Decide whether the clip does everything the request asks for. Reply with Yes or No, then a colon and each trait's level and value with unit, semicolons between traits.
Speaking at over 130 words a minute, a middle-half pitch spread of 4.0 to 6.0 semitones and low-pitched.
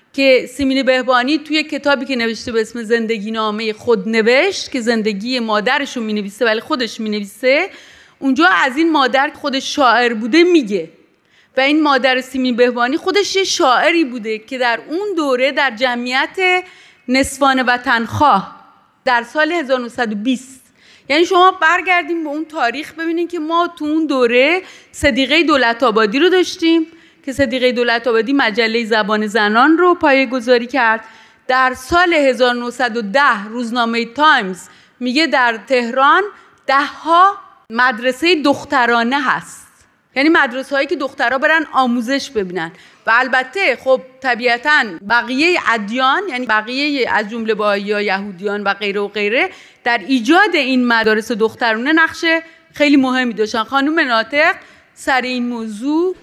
No: average, 140 wpm; average, 4.6 semitones; very high, 260 Hz